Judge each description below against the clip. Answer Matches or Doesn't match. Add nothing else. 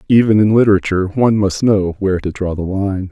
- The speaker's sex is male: Matches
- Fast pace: Matches